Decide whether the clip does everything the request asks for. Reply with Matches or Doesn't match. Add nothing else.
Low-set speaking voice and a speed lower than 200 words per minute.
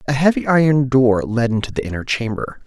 Doesn't match